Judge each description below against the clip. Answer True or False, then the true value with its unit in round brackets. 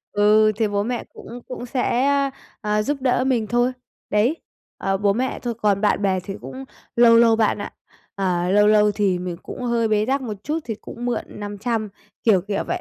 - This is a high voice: True (215 Hz)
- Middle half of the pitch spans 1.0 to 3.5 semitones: True (3.0 semitones)